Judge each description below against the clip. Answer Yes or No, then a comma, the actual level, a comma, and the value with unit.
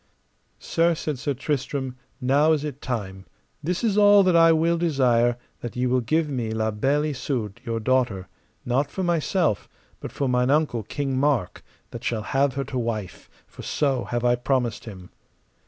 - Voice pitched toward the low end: Yes, low, 130 Hz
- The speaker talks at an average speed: Yes, average, 175 wpm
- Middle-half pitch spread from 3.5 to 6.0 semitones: Yes, average, 4.1 semitones